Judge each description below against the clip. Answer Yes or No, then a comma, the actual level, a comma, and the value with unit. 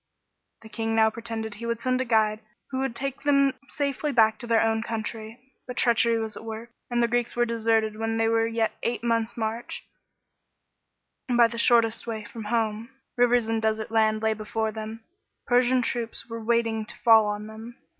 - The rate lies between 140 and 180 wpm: No, average, 190 wpm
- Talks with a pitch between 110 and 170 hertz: No, high, 225 Hz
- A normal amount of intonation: No, narrow, 1.4 semitones